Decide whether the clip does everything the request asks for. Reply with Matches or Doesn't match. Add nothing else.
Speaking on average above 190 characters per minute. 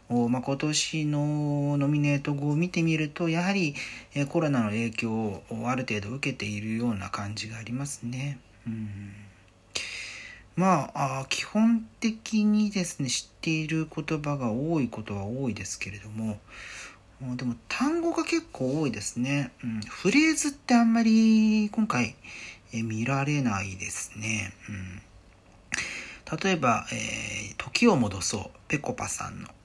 Matches